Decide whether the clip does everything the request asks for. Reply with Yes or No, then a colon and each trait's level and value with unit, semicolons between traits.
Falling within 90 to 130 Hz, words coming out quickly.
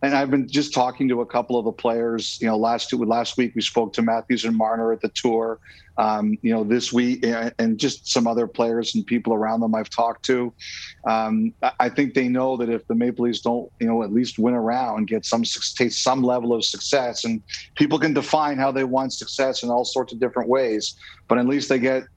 Yes: low, 120 Hz; fast, 235 wpm